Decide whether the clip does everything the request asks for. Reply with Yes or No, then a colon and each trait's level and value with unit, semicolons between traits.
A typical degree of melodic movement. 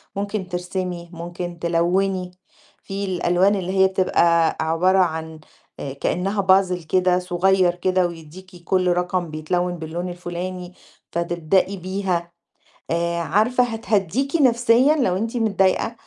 No: narrow, 2.1 semitones